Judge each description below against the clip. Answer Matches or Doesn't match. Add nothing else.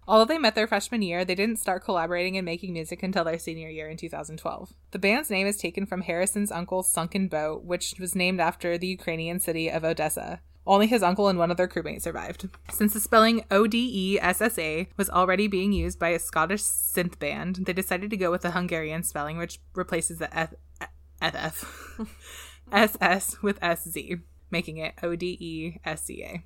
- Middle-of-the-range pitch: Matches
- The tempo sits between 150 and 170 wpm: Doesn't match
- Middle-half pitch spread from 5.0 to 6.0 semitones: Doesn't match